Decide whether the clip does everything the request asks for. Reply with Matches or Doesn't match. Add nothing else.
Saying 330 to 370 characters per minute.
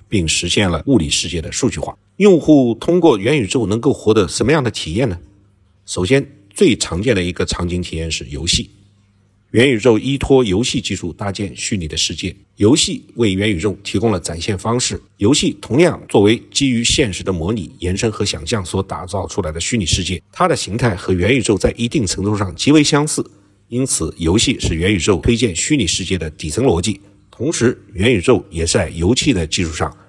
Doesn't match